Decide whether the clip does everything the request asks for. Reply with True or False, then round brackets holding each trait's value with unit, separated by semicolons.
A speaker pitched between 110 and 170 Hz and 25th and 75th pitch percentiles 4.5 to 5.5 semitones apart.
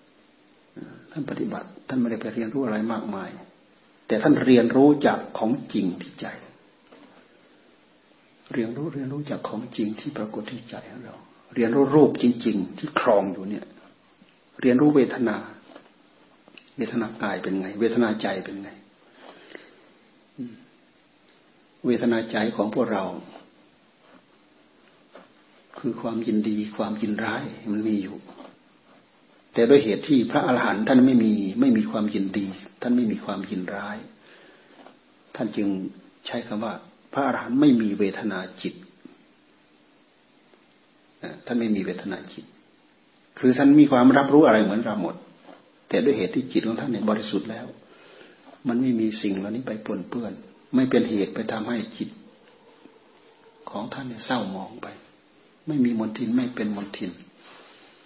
False (115 Hz; 4.0 semitones)